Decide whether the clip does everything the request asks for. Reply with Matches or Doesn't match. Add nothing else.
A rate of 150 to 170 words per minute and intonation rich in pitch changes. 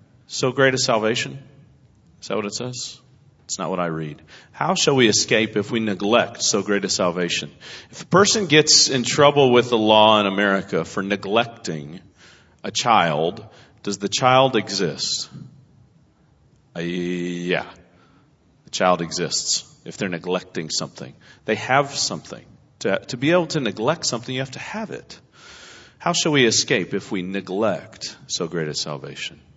Matches